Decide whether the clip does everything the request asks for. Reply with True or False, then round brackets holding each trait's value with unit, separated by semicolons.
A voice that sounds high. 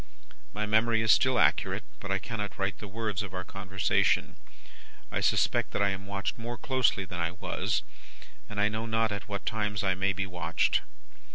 False (100 Hz)